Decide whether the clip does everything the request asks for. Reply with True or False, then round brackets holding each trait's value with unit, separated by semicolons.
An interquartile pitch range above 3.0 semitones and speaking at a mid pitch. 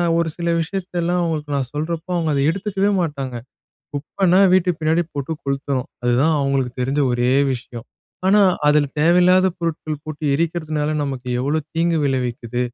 True (3.7 semitones; 155 Hz)